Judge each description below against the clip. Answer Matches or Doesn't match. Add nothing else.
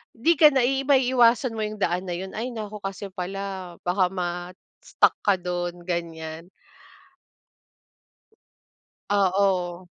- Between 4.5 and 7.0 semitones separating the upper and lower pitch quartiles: Doesn't match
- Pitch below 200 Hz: Matches